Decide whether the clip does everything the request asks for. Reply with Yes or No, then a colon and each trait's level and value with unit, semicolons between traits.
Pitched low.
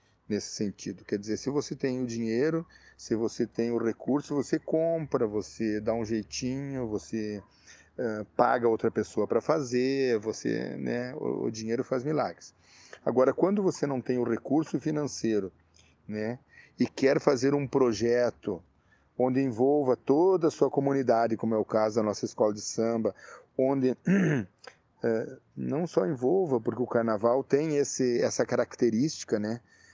Yes: low, 120 Hz